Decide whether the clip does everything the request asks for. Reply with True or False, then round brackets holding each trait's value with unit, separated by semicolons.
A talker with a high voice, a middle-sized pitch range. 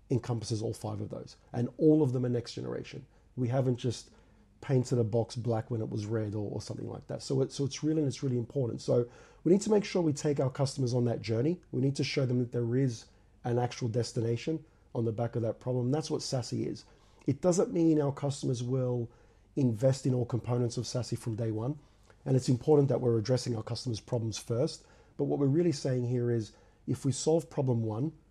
False (125 Hz; 3.3 semitones)